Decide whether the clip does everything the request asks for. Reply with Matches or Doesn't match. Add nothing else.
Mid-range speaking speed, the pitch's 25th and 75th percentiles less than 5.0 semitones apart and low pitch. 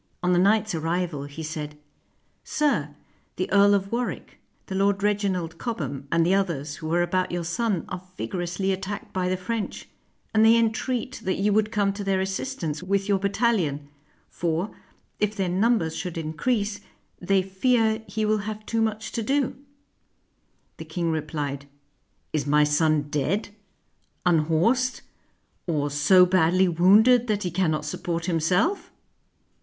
Doesn't match